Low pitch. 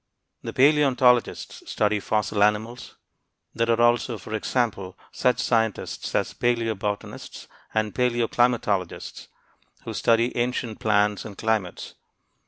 Yes: low, 115 Hz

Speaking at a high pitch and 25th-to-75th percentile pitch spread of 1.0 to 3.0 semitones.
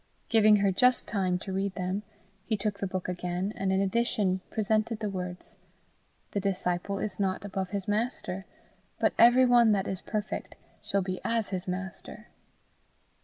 Yes: high, 195 Hz; narrow, 2.4 semitones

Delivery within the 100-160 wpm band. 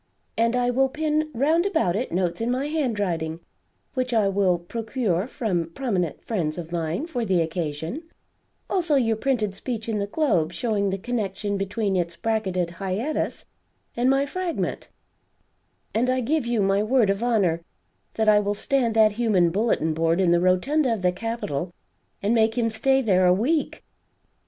No: average, 170 wpm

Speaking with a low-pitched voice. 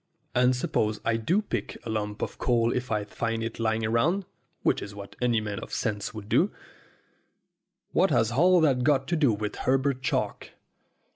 Yes: low, 115 Hz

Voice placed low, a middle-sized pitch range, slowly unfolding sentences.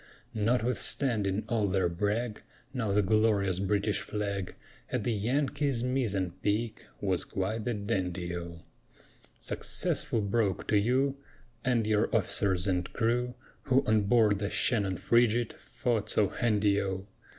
Yes: low, 105 Hz; average, 3.4 semitones; slow, 130 wpm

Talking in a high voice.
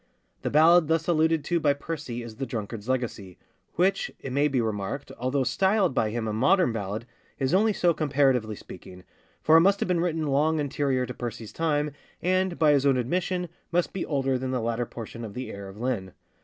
No: low, 135 Hz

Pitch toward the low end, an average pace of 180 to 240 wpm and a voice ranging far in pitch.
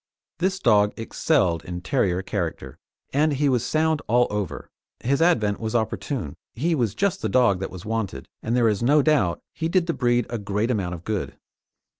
Yes: low, 115 Hz; average, 190 wpm; wide, 6.3 semitones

